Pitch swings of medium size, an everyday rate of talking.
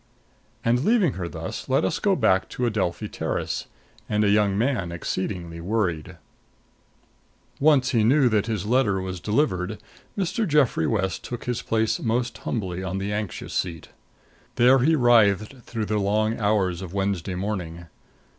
Yes: average, 4.4 semitones; average, 155 wpm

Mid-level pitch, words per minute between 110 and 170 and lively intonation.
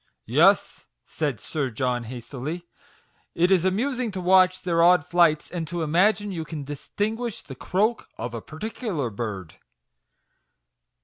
Yes: medium, 170 Hz; average, 160 wpm; wide, 5.8 semitones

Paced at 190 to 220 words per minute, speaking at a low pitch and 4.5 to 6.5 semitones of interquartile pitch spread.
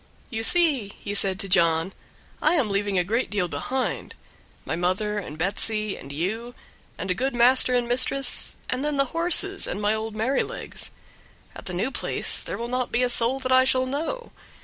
No: average, 195 wpm; high, 230 Hz; average, 4.8 semitones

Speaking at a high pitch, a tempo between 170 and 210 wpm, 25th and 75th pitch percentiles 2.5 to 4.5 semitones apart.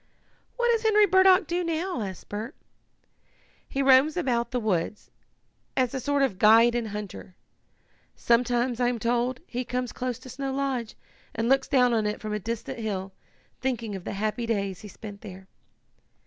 Yes: high, 240 Hz; average, 175 wpm; average, 4.0 semitones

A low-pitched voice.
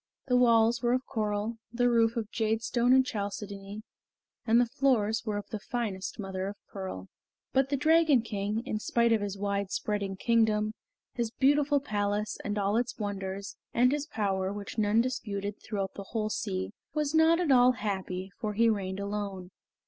No: high, 215 Hz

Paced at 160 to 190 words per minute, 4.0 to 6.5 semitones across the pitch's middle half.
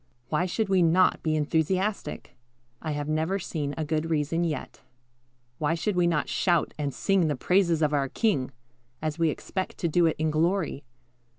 No: average, 180 wpm; average, 3.0 semitones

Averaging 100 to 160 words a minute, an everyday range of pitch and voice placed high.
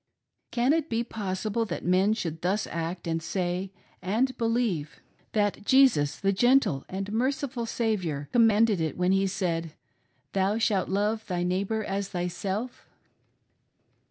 Yes: average, 150 wpm; average, 4.1 semitones; high, 195 Hz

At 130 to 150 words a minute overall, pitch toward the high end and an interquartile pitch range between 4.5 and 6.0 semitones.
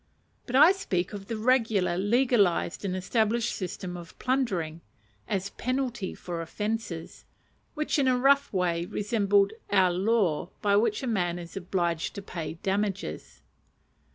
Yes: average, 140 wpm; high, 200 Hz; average, 4.8 semitones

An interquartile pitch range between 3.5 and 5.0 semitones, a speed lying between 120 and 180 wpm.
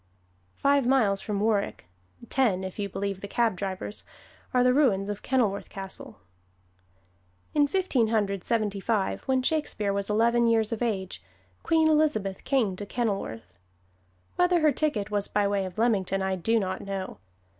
Yes: average, 4.2 semitones; average, 155 wpm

